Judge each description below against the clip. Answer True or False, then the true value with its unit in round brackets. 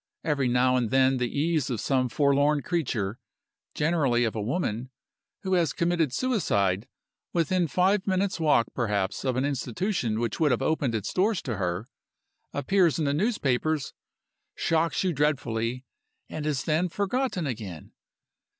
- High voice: False (140 Hz)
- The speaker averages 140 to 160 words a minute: True (150 wpm)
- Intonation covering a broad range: True (5.9 semitones)